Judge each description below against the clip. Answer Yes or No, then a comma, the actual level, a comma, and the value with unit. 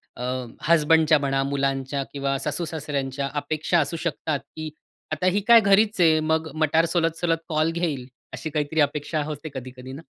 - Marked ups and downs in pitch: No, average, 2.7 semitones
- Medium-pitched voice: Yes, medium, 155 Hz